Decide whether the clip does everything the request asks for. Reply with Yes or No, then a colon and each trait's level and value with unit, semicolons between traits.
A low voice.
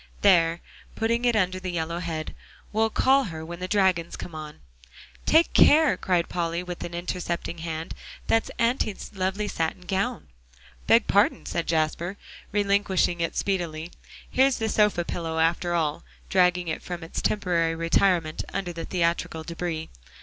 No: medium, 175 Hz